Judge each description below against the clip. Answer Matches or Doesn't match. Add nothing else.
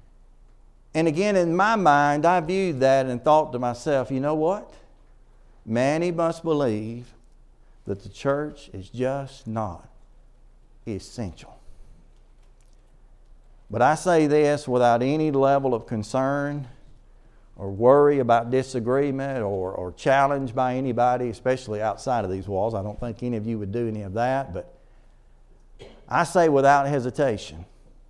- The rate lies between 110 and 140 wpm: Matches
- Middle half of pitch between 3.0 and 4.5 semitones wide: Matches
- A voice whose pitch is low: Matches